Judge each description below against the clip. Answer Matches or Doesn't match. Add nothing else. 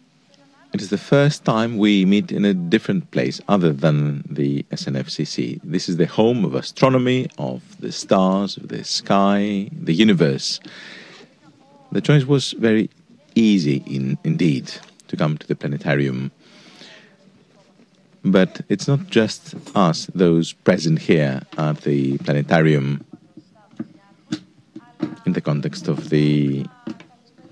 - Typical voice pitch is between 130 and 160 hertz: Doesn't match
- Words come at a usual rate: Matches